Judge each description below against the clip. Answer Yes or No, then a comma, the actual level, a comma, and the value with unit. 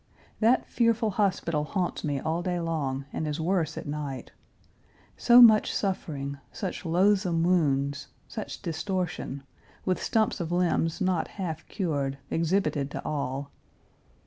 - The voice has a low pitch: No, medium, 170 Hz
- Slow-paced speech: Yes, slow, 130 wpm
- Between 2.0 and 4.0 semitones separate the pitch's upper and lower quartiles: No, average, 4.6 semitones